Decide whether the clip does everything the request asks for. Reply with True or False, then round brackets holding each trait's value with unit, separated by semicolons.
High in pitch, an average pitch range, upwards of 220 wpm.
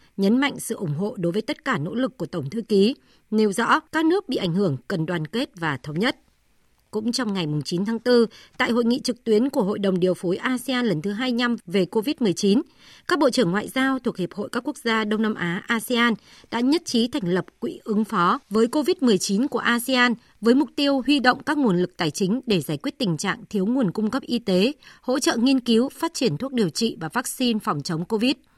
True (225 Hz; 4.7 semitones; 235 wpm)